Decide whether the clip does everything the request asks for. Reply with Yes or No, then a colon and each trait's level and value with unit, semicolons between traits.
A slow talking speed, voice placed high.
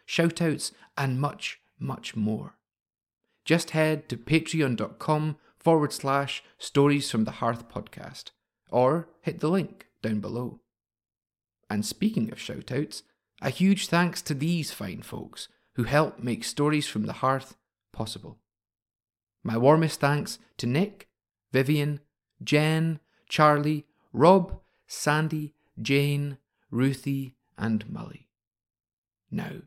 No: slow, 115 wpm; medium, 140 Hz